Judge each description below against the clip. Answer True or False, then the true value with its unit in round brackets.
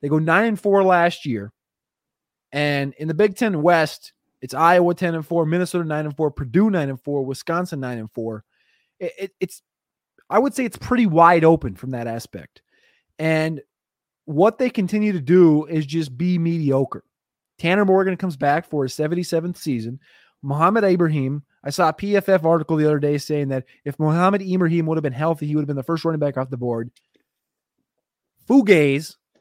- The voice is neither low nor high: True (160 Hz)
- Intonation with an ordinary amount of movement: True (4.0 semitones)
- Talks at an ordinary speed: True (185 wpm)